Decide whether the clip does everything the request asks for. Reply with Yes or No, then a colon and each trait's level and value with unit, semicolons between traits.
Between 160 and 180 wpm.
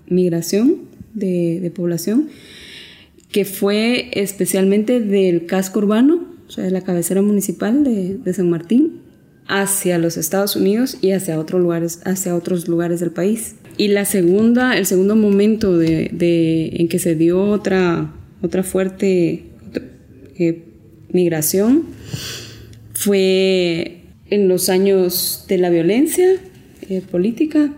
No: average, 130 wpm